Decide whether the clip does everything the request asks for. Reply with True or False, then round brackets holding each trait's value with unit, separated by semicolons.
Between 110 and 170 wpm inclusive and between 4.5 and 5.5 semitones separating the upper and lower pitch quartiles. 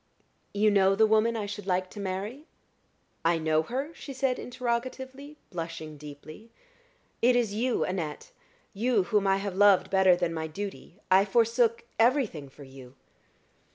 True (155 wpm; 5.2 semitones)